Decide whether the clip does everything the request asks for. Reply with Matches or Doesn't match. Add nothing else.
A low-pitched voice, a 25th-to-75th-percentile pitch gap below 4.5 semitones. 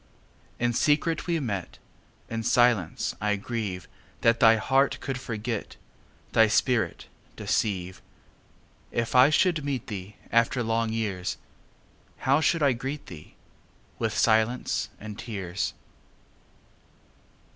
Matches